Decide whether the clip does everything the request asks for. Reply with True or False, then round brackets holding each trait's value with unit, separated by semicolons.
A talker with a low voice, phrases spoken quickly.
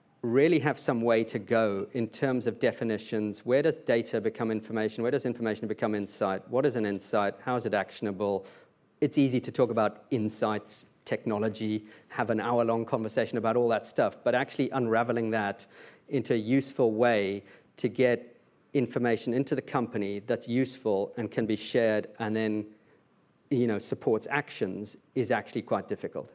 False (115 Hz; 170 wpm)